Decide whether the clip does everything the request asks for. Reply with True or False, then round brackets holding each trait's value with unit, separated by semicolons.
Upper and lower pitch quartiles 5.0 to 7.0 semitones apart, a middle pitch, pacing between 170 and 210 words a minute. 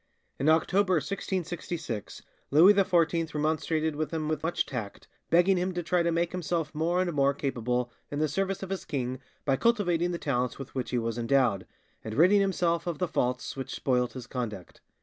True (5.3 semitones; 155 Hz; 190 wpm)